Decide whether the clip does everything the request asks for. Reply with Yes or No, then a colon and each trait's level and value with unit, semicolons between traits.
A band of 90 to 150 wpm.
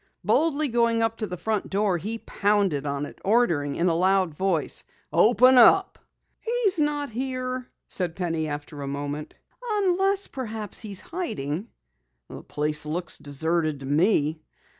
Yes: average, 140 wpm